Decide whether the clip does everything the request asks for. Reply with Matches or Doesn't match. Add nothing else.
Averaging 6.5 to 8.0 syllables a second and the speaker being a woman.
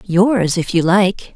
Doesn't match